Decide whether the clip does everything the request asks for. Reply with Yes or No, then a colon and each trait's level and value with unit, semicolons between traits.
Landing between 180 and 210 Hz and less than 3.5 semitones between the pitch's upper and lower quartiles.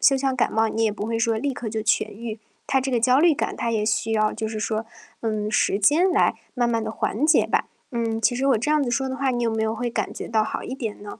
No: high, 230 Hz; average, 3.1 semitones